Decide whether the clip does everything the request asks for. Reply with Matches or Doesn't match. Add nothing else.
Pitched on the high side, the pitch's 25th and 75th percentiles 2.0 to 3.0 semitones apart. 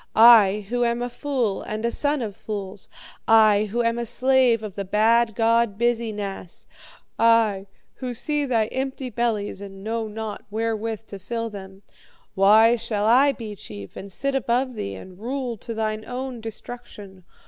Matches